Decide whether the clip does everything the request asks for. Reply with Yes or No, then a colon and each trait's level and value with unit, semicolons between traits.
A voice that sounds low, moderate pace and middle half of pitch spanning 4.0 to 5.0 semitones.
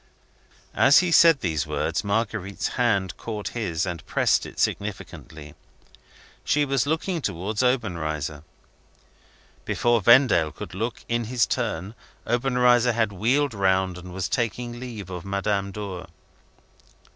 No: low, 105 Hz; slow, 125 wpm; average, 4.6 semitones